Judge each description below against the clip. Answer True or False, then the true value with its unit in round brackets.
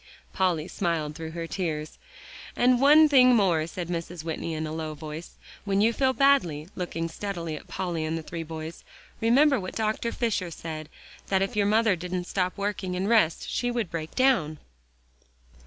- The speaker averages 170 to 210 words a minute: True (175 wpm)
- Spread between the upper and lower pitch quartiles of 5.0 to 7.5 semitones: True (5.3 semitones)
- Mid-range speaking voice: True (180 Hz)